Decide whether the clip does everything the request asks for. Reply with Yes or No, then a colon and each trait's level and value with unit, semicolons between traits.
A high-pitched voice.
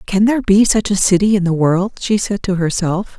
Yes: high, 195 Hz